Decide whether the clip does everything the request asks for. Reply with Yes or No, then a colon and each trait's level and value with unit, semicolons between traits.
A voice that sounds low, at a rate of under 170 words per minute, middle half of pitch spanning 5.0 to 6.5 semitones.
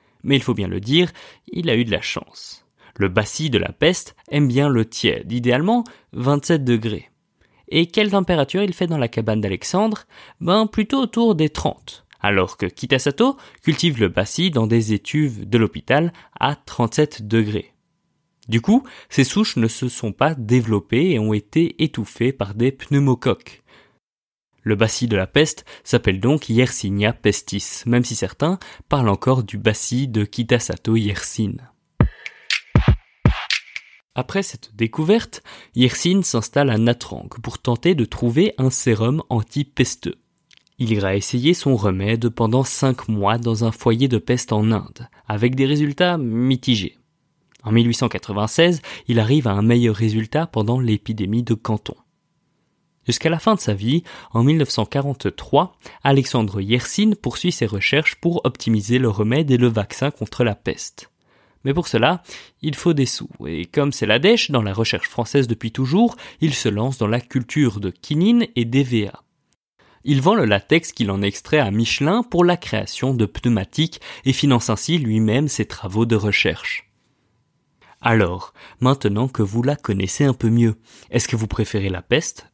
Yes: low, 125 Hz; average, 160 wpm; wide, 5.4 semitones